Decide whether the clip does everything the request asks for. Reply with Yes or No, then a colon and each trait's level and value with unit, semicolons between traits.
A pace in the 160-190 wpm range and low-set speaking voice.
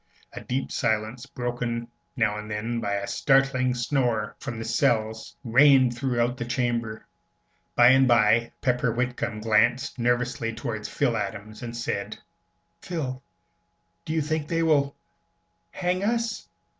No: slow, 135 wpm; low, 120 Hz